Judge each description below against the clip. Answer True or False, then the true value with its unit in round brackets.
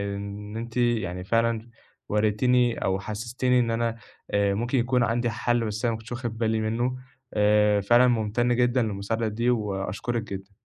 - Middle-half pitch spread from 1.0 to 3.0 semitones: True (2.4 semitones)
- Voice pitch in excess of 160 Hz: False (115 Hz)